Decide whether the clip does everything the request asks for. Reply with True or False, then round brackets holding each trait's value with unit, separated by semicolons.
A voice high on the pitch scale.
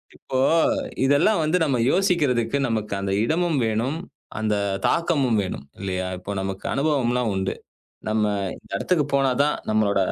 False (125 Hz)